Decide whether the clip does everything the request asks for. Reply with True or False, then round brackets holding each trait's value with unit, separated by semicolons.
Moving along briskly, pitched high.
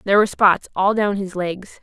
True (230 wpm; 195 Hz)